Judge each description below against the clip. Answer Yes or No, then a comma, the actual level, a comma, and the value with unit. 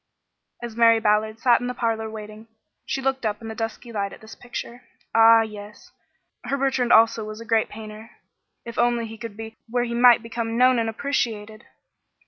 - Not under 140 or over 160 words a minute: No, average, 190 wpm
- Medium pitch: No, high, 225 Hz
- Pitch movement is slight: Yes, narrow, 1.7 semitones